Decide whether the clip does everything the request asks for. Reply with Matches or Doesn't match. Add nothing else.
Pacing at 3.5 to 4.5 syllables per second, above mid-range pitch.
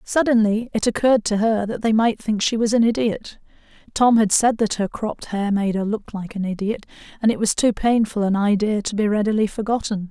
Doesn't match